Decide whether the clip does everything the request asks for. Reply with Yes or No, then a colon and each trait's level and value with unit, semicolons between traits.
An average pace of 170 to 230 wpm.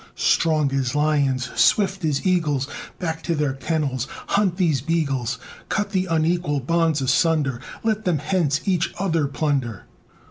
No: average, 140 wpm